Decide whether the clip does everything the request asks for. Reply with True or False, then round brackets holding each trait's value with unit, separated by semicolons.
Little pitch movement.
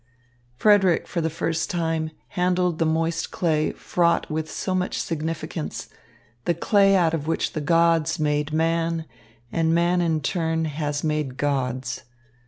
True (1.7 semitones)